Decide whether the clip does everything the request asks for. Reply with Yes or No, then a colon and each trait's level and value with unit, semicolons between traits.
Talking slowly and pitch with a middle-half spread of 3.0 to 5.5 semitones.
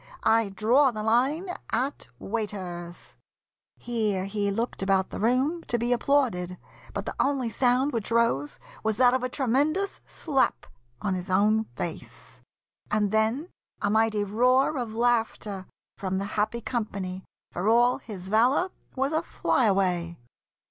No: average, 145 wpm; average, 4.2 semitones